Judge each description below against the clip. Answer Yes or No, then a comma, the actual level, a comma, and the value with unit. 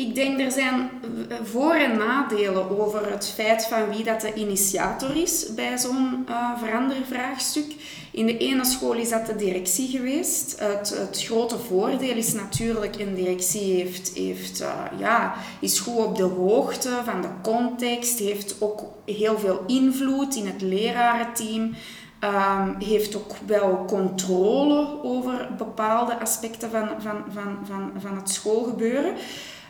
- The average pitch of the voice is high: Yes, high, 225 Hz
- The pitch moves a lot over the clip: No, average, 3.7 semitones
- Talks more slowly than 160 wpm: Yes, average, 145 wpm